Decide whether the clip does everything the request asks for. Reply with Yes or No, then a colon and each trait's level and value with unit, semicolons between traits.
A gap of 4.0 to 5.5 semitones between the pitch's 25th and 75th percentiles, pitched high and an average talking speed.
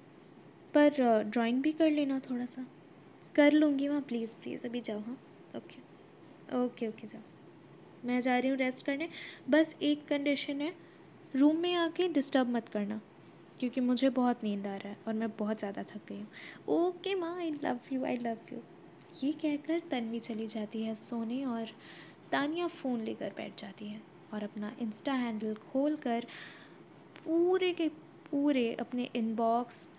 Yes: average, 4.7 semitones; very high, 250 Hz; average, 165 wpm